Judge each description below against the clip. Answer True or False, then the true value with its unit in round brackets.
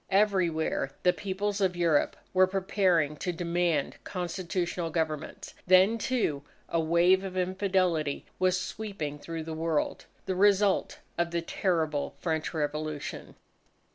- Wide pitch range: False (2.9 semitones)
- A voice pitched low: False (175 Hz)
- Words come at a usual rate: False (125 wpm)